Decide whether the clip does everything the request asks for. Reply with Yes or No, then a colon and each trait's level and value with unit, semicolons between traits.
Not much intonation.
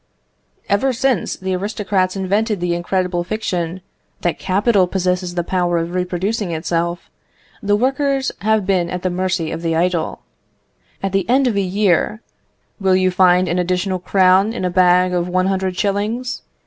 Yes: narrow, 2.3 semitones